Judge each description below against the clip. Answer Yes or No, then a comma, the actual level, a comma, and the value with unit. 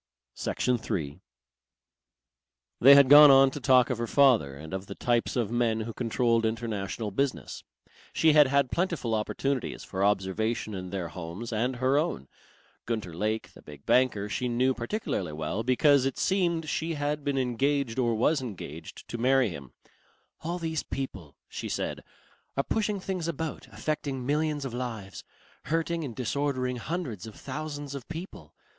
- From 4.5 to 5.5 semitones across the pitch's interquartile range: Yes, average, 5.0 semitones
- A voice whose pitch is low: Yes, low, 125 Hz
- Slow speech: No, average, 160 wpm